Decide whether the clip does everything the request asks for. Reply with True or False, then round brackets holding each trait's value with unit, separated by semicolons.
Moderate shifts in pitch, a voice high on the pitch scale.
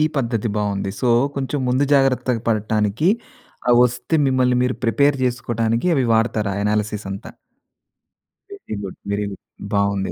False (3.5 semitones; 115 Hz)